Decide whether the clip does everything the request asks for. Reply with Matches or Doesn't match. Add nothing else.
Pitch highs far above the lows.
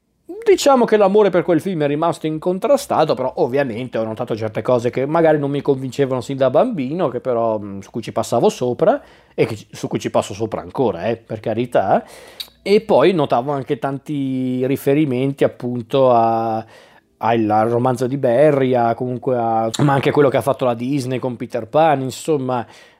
Doesn't match